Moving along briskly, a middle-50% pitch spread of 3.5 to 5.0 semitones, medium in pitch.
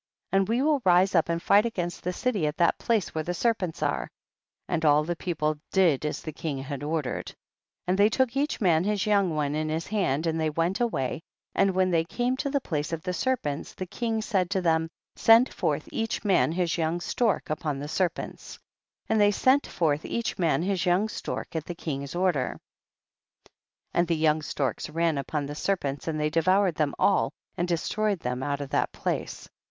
Yes: fast, 210 wpm; average, 4.6 semitones; medium, 170 Hz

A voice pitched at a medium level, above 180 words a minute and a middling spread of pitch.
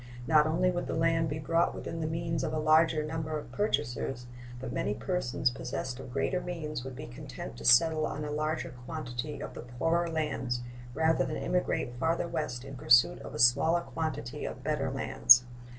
Yes: medium, 150 Hz; average, 190 wpm; average, 4.6 semitones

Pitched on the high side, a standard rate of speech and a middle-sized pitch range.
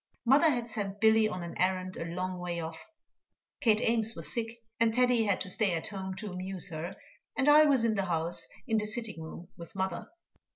No: high, 200 Hz; fast, 210 wpm; average, 4.3 semitones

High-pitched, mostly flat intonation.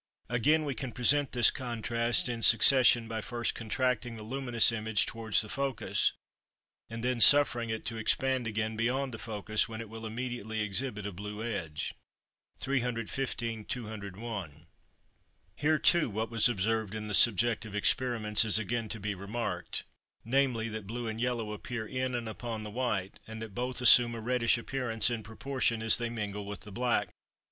No: low, 115 Hz; narrow, 2.2 semitones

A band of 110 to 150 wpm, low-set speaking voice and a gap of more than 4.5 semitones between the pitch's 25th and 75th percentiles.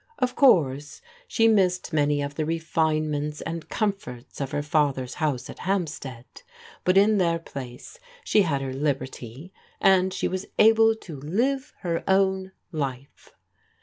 No: average, 145 wpm; medium, 160 Hz; average, 5.2 semitones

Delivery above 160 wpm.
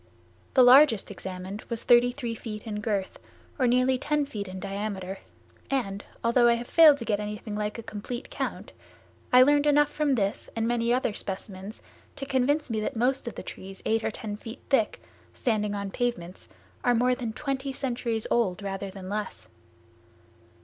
Yes: average, 175 wpm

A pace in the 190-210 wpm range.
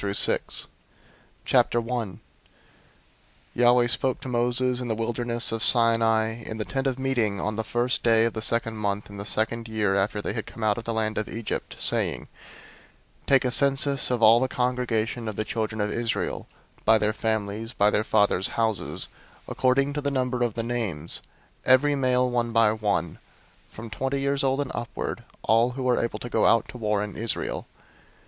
Yes: average, 195 wpm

